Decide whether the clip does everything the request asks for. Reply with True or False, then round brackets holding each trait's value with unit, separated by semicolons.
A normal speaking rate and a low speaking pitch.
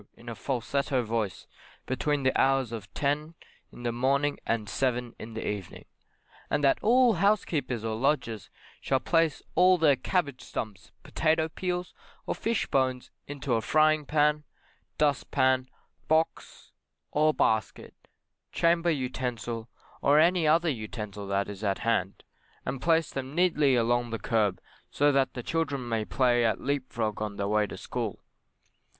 True (150 wpm; 130 Hz)